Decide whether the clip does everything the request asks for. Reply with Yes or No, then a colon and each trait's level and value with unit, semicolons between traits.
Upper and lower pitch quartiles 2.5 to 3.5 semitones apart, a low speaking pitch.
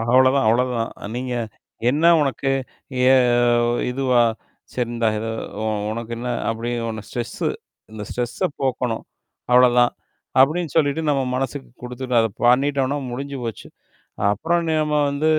Yes: average, 2.9 semitones; low, 125 Hz